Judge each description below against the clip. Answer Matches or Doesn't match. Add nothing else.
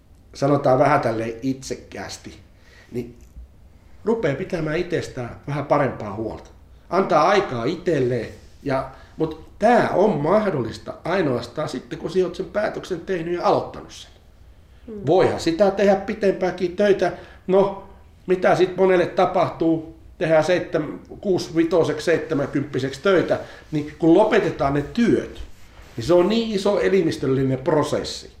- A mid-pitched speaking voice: Matches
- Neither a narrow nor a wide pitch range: Doesn't match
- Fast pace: Doesn't match